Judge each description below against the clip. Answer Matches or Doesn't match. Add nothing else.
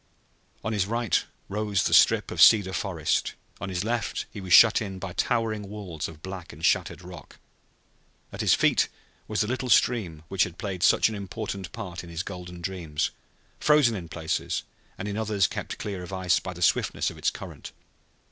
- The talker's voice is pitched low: Matches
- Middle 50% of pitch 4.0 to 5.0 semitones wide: Doesn't match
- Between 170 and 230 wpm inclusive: Matches